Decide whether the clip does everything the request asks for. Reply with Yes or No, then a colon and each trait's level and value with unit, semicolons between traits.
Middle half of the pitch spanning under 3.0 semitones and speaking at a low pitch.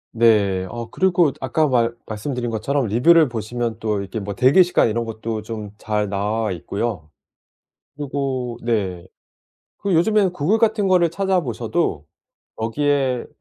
No: wide, 5.6 semitones; low, 120 Hz